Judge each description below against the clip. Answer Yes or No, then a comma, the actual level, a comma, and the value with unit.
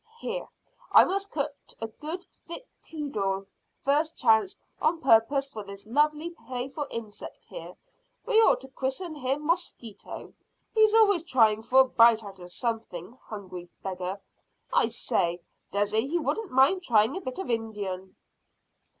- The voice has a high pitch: Yes, very high, 260 Hz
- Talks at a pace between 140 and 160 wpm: Yes, average, 145 wpm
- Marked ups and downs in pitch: Yes, wide, 6.9 semitones